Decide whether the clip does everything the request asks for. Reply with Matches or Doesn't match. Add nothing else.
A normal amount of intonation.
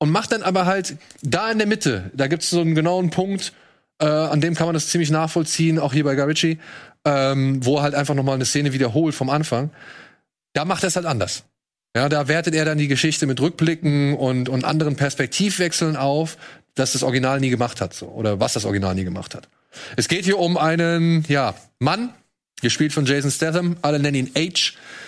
Matches